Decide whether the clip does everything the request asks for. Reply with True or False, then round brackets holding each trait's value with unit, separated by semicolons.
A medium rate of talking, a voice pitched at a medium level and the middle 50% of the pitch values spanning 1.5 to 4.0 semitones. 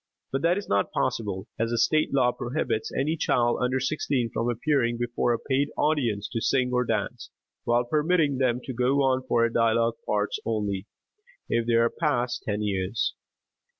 False (175 wpm; 120 Hz; 2.7 semitones)